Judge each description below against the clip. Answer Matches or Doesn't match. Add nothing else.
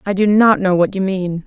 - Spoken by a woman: Matches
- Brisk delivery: Matches